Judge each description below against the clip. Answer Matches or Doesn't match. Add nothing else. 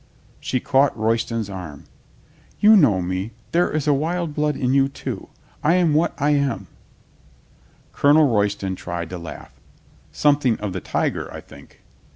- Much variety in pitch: Matches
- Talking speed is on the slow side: Doesn't match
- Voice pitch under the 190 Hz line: Matches